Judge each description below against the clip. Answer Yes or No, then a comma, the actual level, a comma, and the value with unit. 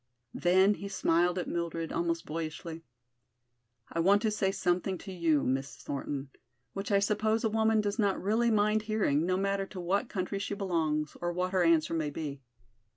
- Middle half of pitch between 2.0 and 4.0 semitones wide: Yes, average, 3.5 semitones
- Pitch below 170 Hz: No, medium, 185 Hz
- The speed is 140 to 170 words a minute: No, average, 180 wpm